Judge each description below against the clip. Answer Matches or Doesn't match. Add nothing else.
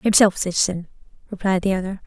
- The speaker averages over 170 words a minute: Doesn't match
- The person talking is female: Matches